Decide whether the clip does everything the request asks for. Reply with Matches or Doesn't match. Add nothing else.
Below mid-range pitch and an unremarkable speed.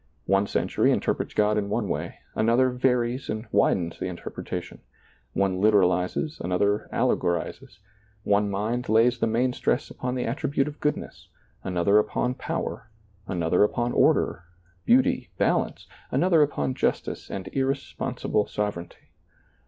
Doesn't match